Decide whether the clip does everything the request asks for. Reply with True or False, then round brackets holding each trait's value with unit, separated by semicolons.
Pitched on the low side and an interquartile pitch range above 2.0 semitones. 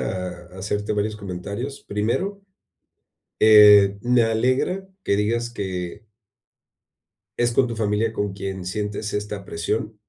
True (105 Hz; 2.5 semitones)